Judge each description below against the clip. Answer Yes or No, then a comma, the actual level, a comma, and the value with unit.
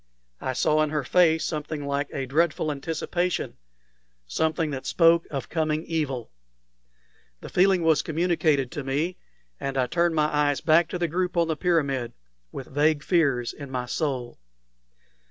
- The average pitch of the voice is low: No, medium, 155 Hz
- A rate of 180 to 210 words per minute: No, average, 155 wpm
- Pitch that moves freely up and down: No, average, 3.4 semitones